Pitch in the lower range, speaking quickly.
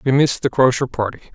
Yes: low, 125 Hz; fast, 225 wpm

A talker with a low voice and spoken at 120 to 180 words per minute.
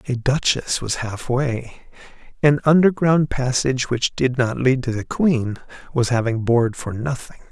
Yes: low, 130 Hz; average, 150 wpm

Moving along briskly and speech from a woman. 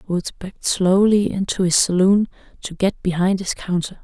No: average, 165 wpm; female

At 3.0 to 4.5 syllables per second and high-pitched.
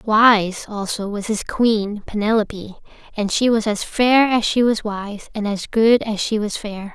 Yes: 4.1 syllables/s; high, 215 Hz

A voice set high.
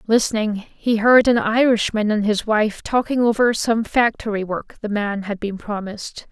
Yes: high, 220 Hz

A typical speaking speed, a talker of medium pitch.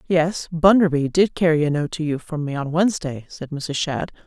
No: fast, 210 wpm; medium, 160 Hz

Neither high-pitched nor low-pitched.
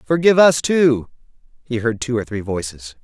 No: low, 125 Hz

